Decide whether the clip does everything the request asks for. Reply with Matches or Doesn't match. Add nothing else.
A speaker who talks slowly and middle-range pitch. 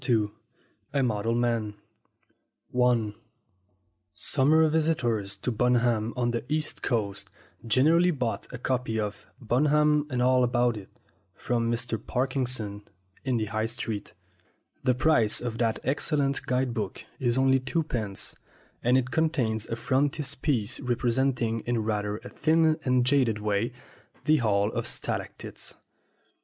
Doesn't match